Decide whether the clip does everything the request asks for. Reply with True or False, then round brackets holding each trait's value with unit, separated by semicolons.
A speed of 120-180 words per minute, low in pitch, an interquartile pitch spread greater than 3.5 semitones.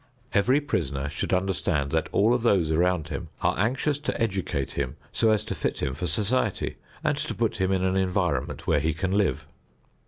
False (195 wpm; 95 Hz; 5.3 semitones)